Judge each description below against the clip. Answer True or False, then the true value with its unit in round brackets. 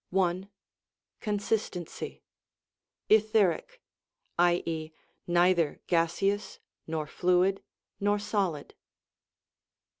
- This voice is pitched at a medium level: True (180 Hz)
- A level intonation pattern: False (3.2 semitones)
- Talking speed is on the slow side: True (60 wpm)